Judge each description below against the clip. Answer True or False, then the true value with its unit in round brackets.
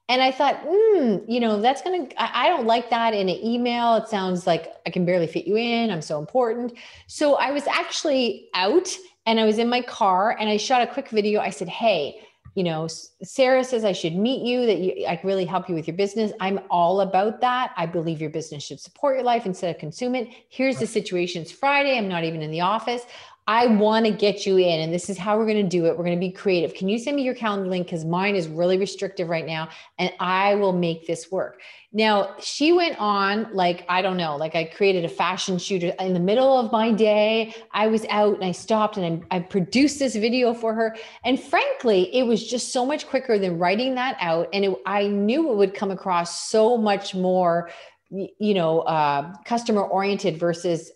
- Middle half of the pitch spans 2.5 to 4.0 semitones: False (4.9 semitones)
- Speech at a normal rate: False (230 wpm)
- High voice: True (205 Hz)